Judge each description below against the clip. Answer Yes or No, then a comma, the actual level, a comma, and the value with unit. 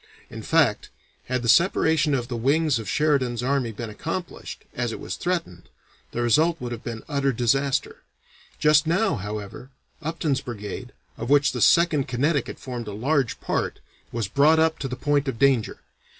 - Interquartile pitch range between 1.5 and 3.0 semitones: No, average, 4.3 semitones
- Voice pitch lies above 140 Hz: No, low, 135 Hz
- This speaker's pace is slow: No, average, 170 wpm